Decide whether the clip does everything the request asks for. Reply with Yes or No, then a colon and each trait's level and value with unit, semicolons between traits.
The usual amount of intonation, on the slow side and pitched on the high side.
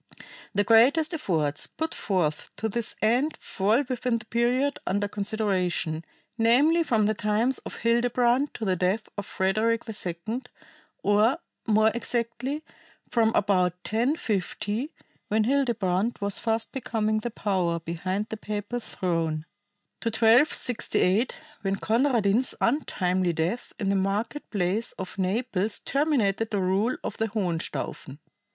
Yes: average, 3.8 semitones; slow, 130 wpm; high, 215 Hz